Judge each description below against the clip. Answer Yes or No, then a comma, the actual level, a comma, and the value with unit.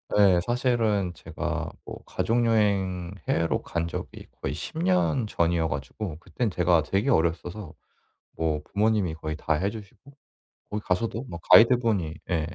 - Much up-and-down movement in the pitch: No, average, 4.6 semitones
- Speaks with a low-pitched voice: Yes, very low, 95 Hz